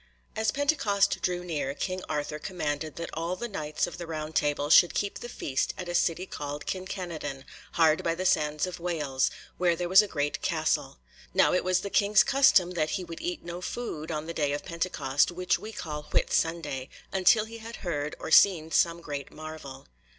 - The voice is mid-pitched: Yes, medium, 170 Hz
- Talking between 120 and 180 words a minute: No, average, 200 wpm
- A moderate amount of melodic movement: Yes, average, 3.6 semitones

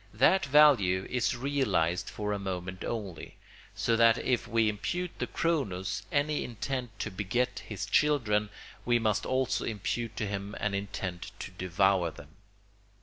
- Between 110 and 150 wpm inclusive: Yes, average, 145 wpm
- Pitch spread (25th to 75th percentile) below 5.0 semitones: Yes, average, 4.5 semitones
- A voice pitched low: Yes, low, 105 Hz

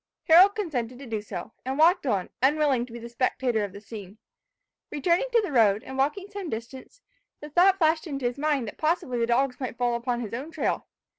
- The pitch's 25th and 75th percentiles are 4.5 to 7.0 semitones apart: Yes, average, 5.0 semitones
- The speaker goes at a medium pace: No, fast, 215 wpm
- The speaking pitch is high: Yes, very high, 265 Hz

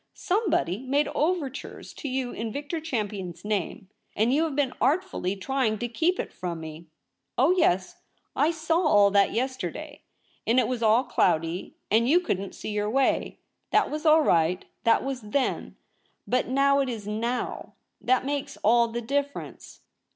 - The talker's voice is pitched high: Yes, very high, 250 Hz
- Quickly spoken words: No, average, 165 wpm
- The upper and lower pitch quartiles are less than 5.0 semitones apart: No, wide, 5.4 semitones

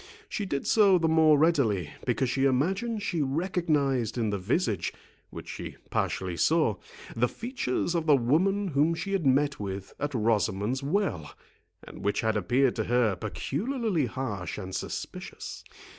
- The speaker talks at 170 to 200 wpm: No, average, 155 wpm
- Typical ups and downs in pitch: No, wide, 7.4 semitones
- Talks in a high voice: No, low, 135 Hz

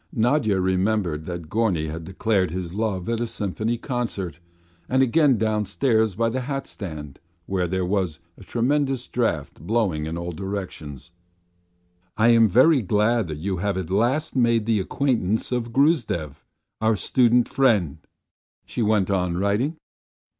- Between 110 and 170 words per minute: Yes, average, 145 wpm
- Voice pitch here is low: Yes, low, 105 Hz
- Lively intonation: No, average, 4.6 semitones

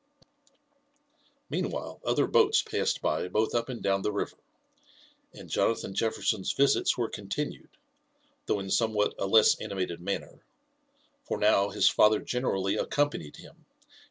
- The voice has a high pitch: No, low, 105 Hz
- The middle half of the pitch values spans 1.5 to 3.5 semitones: Yes, average, 3.2 semitones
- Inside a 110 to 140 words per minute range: Yes, slow, 135 wpm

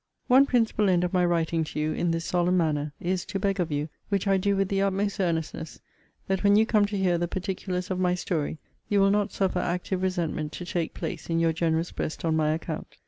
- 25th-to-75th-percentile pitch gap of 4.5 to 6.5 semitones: No, average, 3.0 semitones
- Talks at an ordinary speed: No, fast, 235 wpm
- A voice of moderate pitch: Yes, medium, 180 Hz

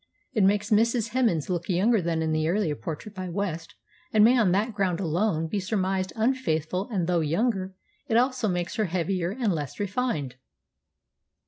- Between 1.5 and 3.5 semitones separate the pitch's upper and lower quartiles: No, average, 4.3 semitones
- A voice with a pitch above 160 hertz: Yes, high, 190 Hz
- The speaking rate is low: No, average, 175 wpm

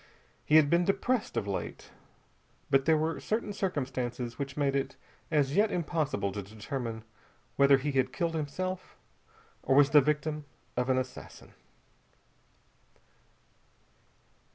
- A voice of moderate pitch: Yes, medium, 145 Hz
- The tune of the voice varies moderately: Yes, average, 3.9 semitones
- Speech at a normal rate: No, slow, 130 wpm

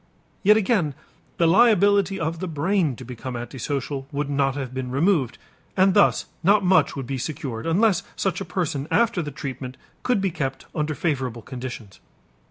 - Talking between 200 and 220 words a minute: No, average, 170 wpm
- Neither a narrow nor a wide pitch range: No, wide, 6.2 semitones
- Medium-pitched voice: Yes, medium, 150 Hz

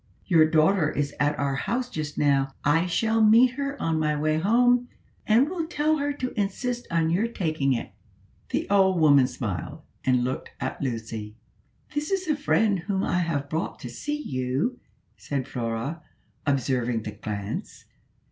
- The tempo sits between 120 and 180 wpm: Yes, average, 165 wpm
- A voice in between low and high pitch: Yes, medium, 160 Hz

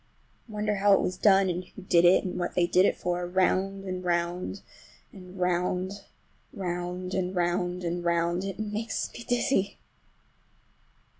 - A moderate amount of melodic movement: No, narrow, 1.7 semitones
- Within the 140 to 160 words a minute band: Yes, average, 150 wpm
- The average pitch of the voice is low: No, medium, 180 Hz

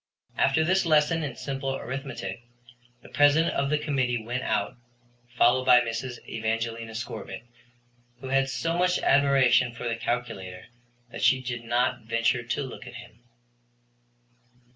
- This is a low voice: Yes, low, 125 Hz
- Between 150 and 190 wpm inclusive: No, average, 140 wpm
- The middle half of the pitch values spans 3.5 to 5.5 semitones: No, average, 3.1 semitones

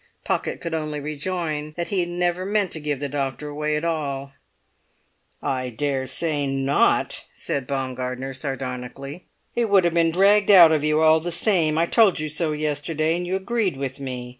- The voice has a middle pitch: Yes, medium, 155 Hz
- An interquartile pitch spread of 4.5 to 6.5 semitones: No, average, 3.9 semitones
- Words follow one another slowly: No, average, 180 wpm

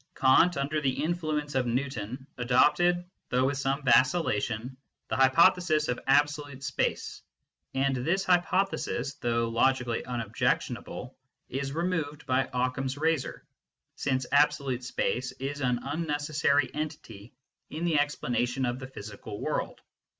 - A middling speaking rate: No, slow, 130 wpm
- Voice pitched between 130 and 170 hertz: Yes, low, 135 Hz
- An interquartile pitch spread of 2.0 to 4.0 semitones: Yes, average, 3.1 semitones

